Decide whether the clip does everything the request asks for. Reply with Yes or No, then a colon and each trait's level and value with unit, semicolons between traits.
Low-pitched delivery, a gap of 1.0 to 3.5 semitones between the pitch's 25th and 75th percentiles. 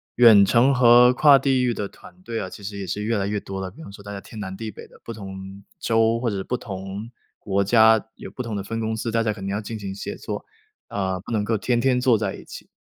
Yes: low, 110 Hz; average, 3.0 semitones